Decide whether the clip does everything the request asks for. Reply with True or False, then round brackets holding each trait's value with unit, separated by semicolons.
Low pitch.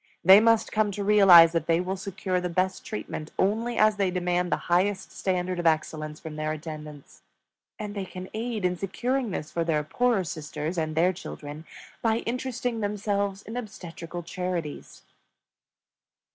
False (185 Hz)